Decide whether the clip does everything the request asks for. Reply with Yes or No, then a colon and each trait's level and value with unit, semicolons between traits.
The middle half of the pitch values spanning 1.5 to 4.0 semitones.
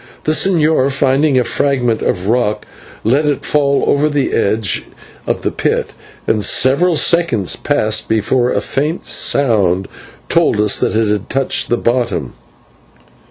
No: average, 4.9 semitones